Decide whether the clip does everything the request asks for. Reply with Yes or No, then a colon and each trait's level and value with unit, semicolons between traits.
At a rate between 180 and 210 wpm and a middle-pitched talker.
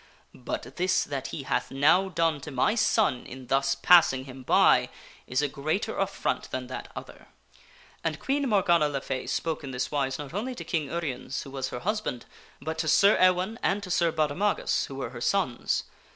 Yes: average, 195 wpm; medium, 150 Hz